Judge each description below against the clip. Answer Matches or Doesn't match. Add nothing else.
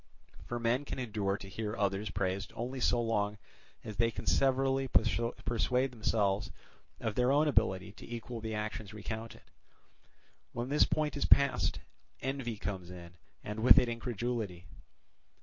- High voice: Doesn't match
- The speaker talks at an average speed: Matches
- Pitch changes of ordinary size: Matches